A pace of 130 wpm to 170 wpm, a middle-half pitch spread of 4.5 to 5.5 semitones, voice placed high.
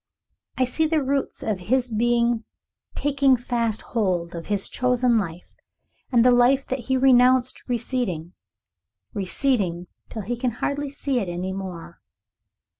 Yes: average, 140 wpm; average, 4.9 semitones; high, 240 Hz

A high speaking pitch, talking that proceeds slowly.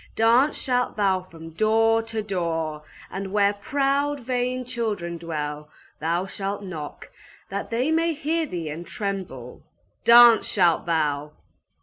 Yes: high, 200 Hz; slow, 130 wpm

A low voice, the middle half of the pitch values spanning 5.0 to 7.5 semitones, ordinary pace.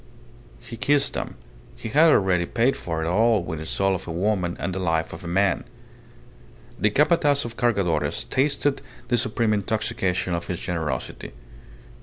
Yes: low, 100 Hz; average, 5.3 semitones; average, 165 wpm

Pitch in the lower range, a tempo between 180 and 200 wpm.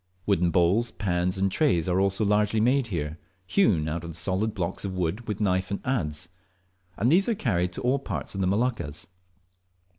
Yes: very low, 95 Hz; average, 185 wpm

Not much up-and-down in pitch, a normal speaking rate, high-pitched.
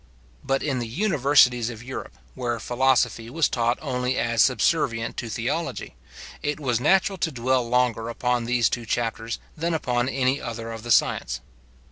No: narrow, 2.3 semitones; average, 160 wpm; low, 125 Hz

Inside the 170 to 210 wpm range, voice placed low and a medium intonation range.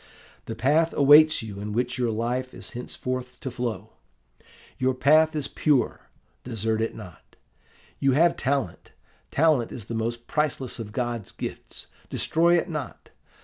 No: average, 145 wpm; low, 125 Hz; average, 4.2 semitones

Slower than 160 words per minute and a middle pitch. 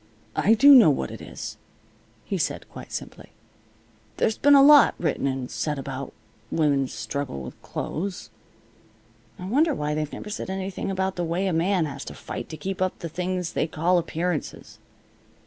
No: average, 175 wpm; medium, 175 Hz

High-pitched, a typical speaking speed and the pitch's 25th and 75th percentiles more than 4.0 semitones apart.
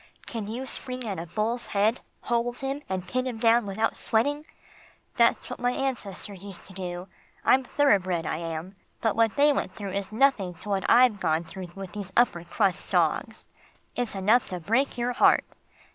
Yes: high, 210 Hz; average, 185 wpm; average, 4.6 semitones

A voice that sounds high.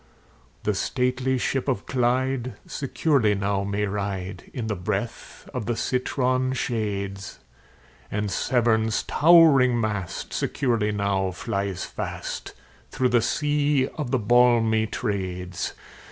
No: low, 115 Hz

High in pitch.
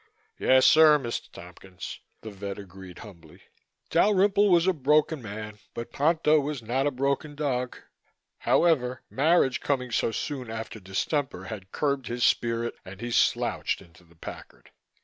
No: low, 125 Hz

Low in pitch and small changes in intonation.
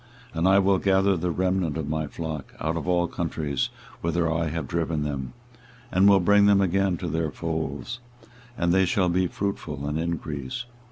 No: very low, 85 Hz; average, 3.2 semitones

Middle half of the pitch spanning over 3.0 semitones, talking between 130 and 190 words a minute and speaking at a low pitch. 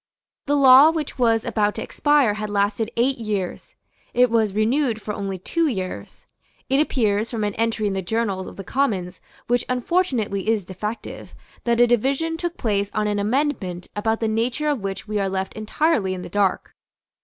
No: average, 4.2 semitones; average, 185 wpm; high, 220 Hz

